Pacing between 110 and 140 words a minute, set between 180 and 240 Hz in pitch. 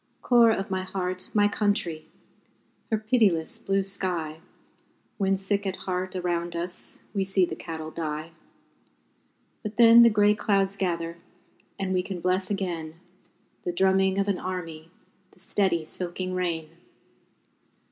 Yes: slow, 135 wpm; medium, 185 Hz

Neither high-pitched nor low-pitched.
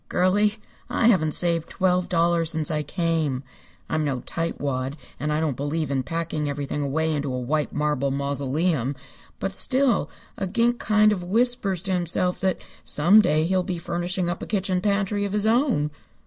Yes: medium, 170 Hz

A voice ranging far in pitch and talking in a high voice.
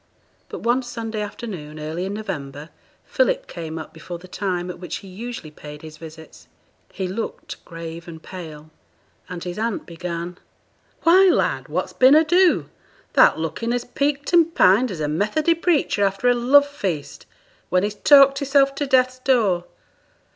Yes: wide, 7.7 semitones; high, 200 Hz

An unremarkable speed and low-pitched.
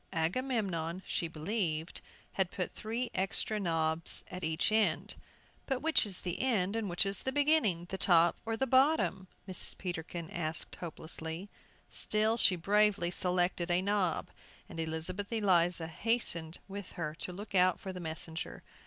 No: average, 155 wpm; medium, 185 Hz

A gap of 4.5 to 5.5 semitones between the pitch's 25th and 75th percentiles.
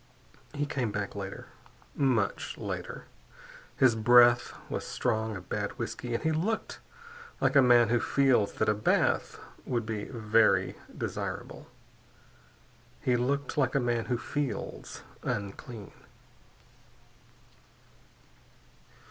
No: average, 3.4 semitones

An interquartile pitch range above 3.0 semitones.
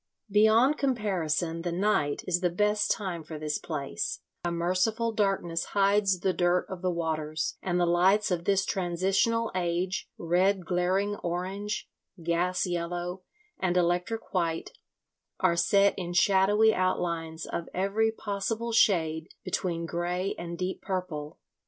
No: average, 2.7 semitones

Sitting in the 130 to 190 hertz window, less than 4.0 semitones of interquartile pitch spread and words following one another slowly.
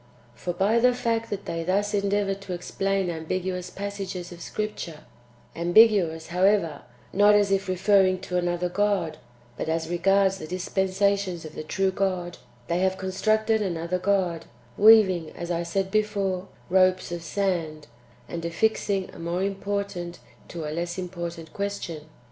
No: medium, 185 Hz; narrow, 2.6 semitones; average, 150 wpm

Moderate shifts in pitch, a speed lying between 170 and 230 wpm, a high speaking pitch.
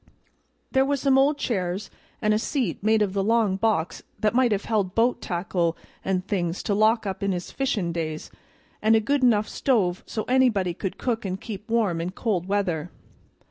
Yes: average, 4.0 semitones; average, 190 wpm; high, 210 Hz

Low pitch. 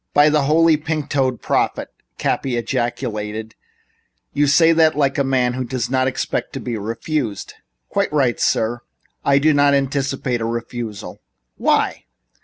Yes: low, 130 Hz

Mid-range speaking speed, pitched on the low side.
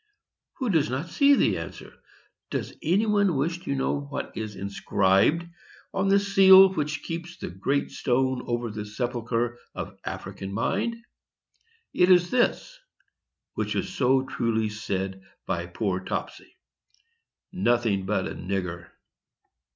No: slow, 130 wpm; low, 130 Hz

